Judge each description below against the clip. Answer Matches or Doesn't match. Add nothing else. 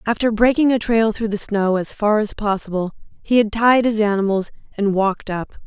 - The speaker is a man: Doesn't match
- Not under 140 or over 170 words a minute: Doesn't match